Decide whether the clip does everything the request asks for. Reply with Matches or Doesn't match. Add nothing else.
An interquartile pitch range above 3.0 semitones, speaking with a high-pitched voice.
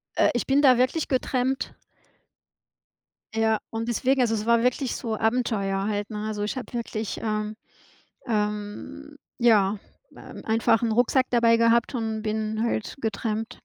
Doesn't match